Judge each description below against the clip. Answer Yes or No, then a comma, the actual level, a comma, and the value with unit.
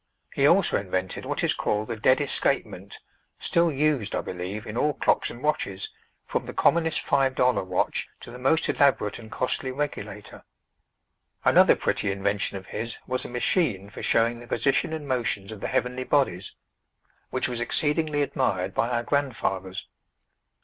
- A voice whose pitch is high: No, low, 120 Hz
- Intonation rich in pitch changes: Yes, wide, 5.7 semitones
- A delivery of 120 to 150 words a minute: No, average, 165 wpm